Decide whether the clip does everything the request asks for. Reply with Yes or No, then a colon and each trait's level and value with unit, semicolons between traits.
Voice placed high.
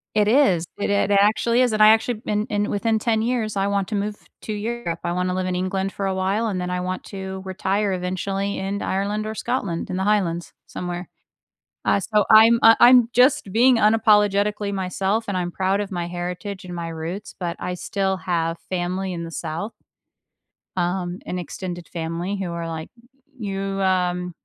Yes: high, 195 Hz